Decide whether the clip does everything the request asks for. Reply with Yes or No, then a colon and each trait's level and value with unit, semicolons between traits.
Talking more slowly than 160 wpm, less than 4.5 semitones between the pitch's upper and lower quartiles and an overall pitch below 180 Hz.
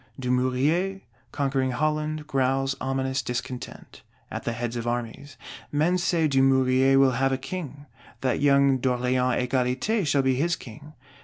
Yes: average, 140 wpm; narrow, 2.4 semitones; low, 135 Hz